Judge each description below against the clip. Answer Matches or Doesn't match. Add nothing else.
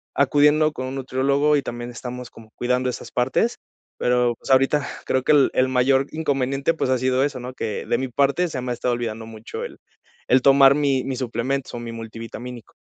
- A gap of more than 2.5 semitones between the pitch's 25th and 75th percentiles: Doesn't match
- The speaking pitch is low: Matches